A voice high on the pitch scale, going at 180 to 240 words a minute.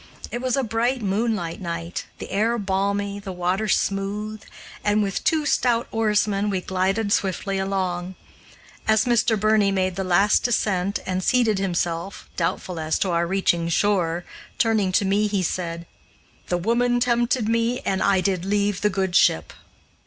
No: high, 200 Hz; average, 160 wpm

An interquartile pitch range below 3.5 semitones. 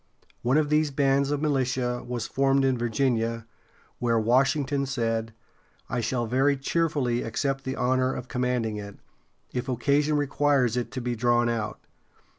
Yes: narrow, 2.5 semitones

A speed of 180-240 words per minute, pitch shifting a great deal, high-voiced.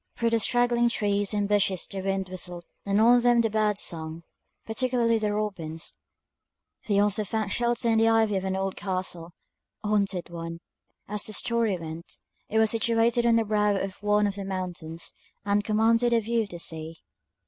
No: average, 185 wpm; average, 3.3 semitones; high, 205 Hz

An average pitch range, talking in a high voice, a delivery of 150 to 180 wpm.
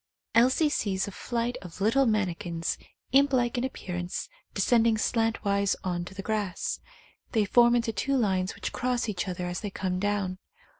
Yes: average, 4.3 semitones; high, 210 Hz; average, 170 wpm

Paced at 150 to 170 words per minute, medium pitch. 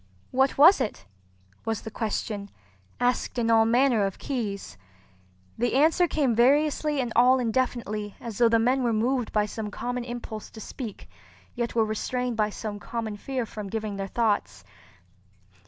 No: average, 160 wpm; high, 230 Hz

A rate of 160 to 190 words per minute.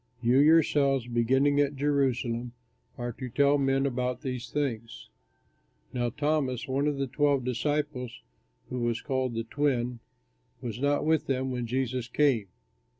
No: average, 145 wpm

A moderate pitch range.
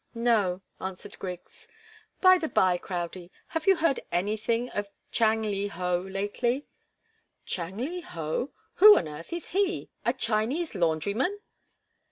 No: wide, 7.1 semitones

